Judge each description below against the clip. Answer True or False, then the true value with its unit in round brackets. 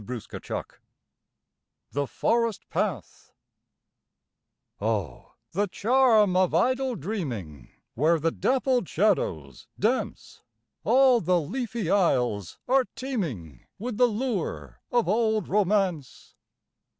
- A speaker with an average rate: False (95 wpm)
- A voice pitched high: True (195 Hz)